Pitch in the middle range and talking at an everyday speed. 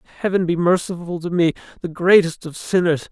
Yes: medium, 175 Hz; average, 175 wpm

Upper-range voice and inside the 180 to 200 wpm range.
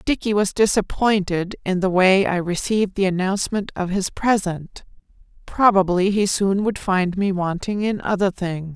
No: high, 195 Hz; average, 160 wpm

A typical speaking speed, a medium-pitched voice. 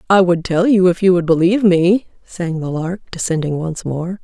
No: fast, 215 wpm; medium, 175 Hz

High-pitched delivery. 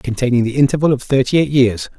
No: low, 130 Hz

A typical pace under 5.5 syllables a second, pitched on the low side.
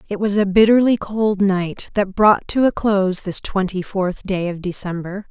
No: 4.5 syllables/s; high, 195 Hz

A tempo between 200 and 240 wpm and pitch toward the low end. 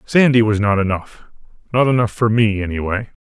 No: average, 170 wpm; low, 110 Hz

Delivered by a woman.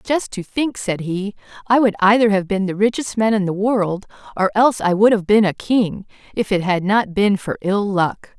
Yes: female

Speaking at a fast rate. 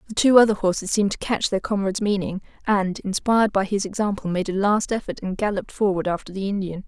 Yes: fast, 220 wpm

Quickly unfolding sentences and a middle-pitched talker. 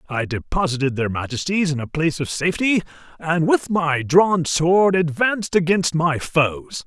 No: average, 155 wpm; medium, 160 Hz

